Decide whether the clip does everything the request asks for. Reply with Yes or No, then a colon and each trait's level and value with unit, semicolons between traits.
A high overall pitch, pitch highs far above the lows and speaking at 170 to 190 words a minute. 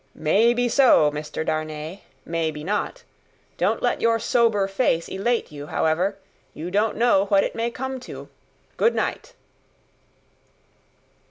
No: high, 200 Hz; wide, 6.8 semitones; average, 140 wpm